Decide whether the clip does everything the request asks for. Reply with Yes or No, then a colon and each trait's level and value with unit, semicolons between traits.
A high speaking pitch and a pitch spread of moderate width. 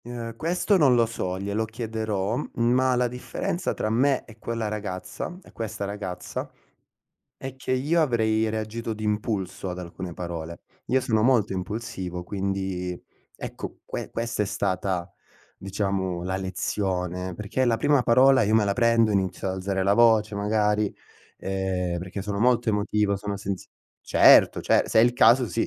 No: low, 105 Hz; average, 3.4 semitones